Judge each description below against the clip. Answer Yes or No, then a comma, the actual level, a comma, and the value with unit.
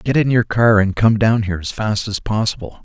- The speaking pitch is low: Yes, low, 110 Hz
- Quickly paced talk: Yes, fast, 255 wpm